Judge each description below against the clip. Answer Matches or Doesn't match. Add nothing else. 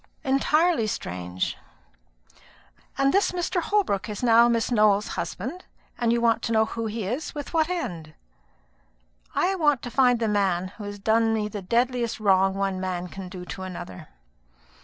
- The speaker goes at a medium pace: Matches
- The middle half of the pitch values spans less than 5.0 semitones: Doesn't match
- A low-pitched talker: Doesn't match